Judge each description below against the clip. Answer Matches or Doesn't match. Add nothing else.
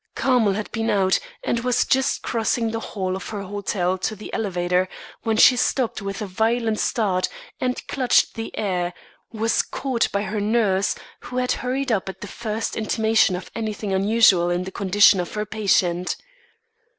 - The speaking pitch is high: Matches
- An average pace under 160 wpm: Doesn't match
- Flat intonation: Doesn't match